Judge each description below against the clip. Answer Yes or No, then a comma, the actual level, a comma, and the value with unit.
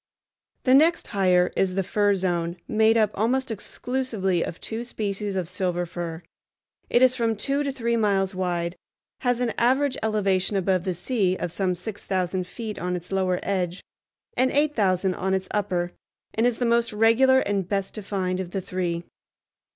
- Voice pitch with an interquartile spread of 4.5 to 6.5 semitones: No, average, 4.0 semitones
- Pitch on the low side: No, high, 195 Hz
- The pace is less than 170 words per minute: No, average, 175 wpm